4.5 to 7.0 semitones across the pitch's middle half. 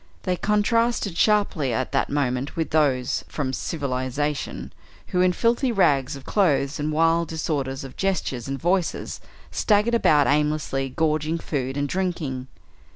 Yes: average, 5.0 semitones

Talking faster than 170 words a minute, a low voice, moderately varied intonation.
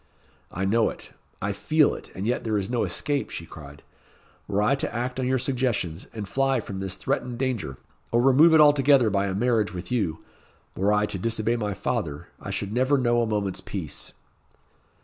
Yes: average, 195 wpm; low, 115 Hz; average, 4.8 semitones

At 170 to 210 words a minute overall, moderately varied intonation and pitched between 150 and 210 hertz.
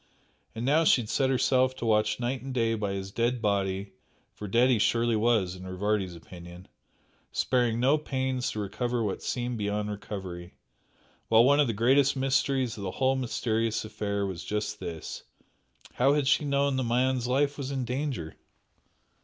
No: average, 175 wpm; average, 4.2 semitones; low, 115 Hz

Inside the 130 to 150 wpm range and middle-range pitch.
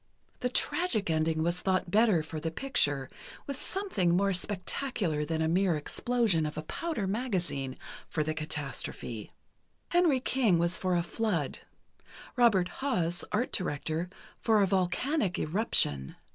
Yes: average, 140 wpm; medium, 180 Hz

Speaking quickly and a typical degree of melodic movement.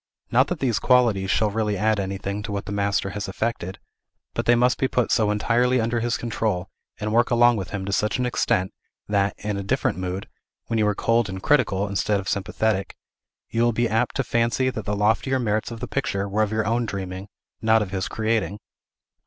Yes: fast, 215 wpm; average, 3.0 semitones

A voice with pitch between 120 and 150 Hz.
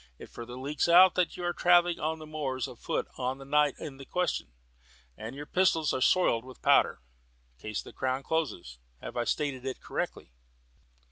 Yes: medium, 140 Hz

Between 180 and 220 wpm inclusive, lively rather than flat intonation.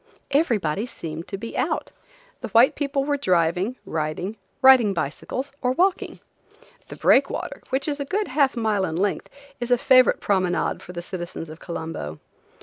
No: average, 160 wpm; wide, 7.4 semitones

